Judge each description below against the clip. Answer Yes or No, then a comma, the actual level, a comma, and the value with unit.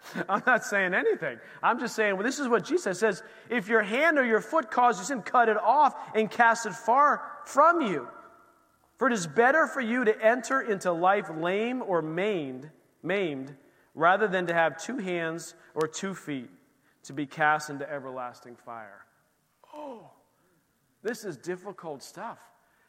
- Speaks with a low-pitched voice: No, high, 215 Hz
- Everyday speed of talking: Yes, average, 170 wpm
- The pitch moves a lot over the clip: Yes, wide, 7.4 semitones